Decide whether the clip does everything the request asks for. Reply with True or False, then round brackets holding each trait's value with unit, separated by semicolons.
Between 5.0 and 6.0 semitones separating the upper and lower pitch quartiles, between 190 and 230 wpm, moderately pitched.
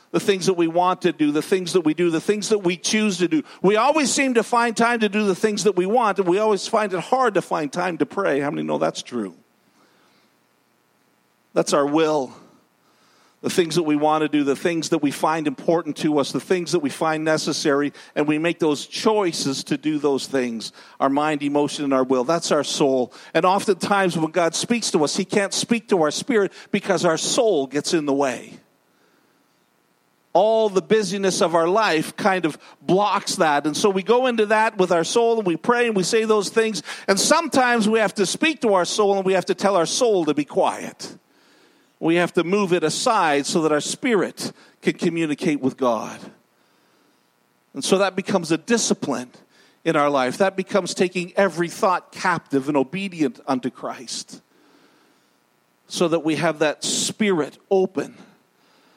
True (5.5 semitones; 200 wpm; 175 Hz)